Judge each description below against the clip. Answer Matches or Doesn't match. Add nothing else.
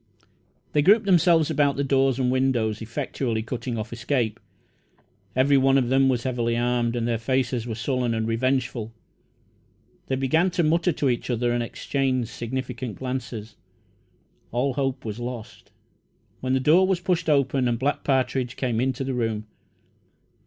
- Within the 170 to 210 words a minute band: Doesn't match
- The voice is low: Matches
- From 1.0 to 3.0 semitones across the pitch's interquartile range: Matches